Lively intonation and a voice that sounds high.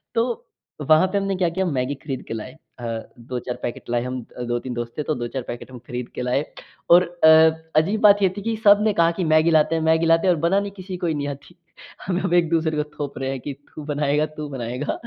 No: wide, 5.8 semitones; medium, 155 Hz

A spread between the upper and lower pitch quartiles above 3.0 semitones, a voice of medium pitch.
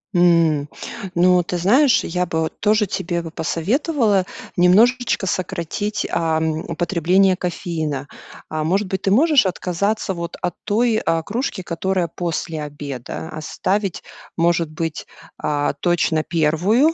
Yes: average, 3.7 semitones; medium, 175 Hz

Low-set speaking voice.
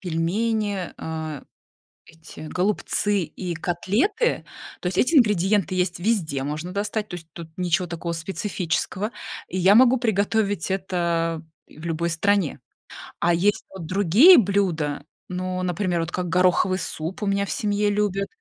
No: medium, 185 Hz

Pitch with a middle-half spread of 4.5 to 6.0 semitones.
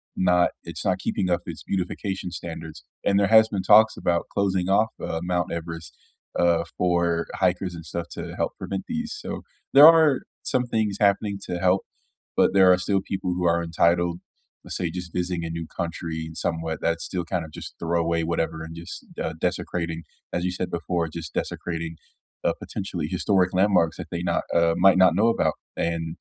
No: narrow, 2.4 semitones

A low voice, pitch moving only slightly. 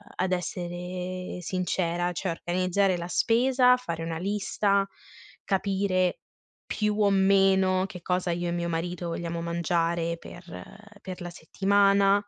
No: medium, 185 Hz; narrow, 2.2 semitones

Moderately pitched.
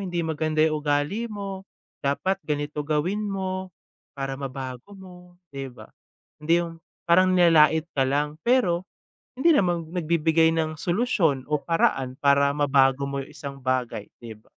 Yes: medium, 155 Hz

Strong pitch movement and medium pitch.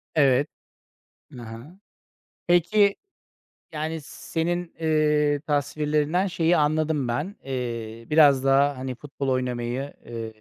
No: average, 3.7 semitones; medium, 145 Hz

